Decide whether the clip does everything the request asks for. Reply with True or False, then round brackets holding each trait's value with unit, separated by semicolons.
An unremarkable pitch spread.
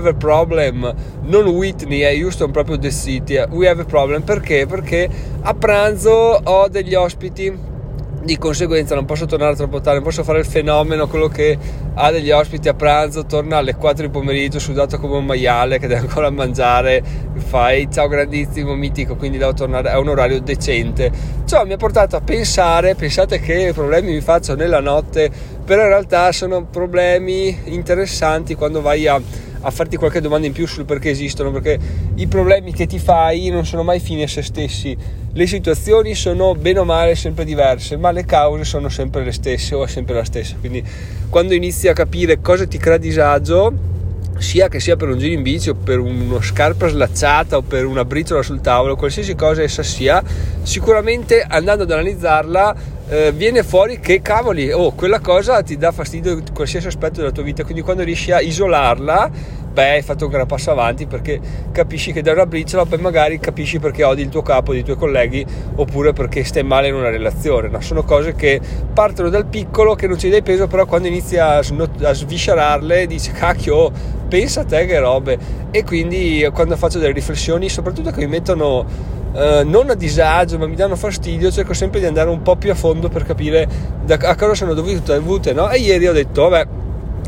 True (4.7 semitones)